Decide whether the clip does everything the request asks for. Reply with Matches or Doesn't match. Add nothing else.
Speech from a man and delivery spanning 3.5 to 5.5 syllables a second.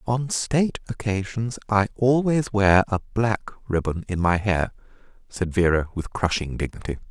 Matches